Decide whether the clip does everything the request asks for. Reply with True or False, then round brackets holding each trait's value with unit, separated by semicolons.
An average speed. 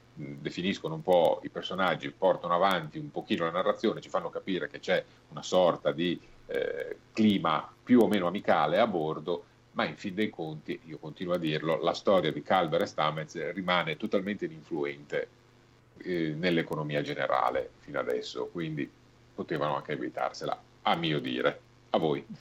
True (160 wpm)